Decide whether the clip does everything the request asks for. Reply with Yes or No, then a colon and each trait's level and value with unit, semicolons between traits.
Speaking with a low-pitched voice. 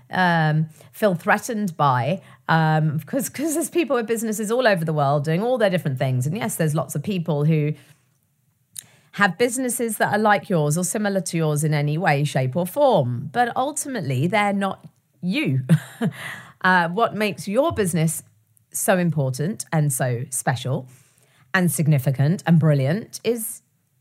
No: medium, 160 Hz